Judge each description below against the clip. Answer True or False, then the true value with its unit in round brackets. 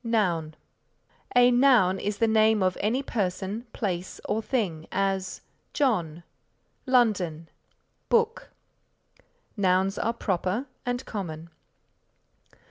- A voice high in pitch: True (205 Hz)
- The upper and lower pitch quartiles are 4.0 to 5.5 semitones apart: True (4.5 semitones)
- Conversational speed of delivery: False (100 wpm)